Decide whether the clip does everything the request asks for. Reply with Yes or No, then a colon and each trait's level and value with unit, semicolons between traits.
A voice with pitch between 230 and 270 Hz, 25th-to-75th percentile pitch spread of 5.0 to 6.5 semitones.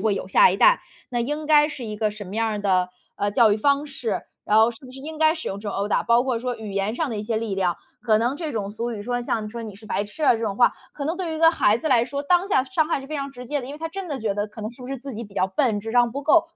Yes: high, 240 Hz; wide, 5.4 semitones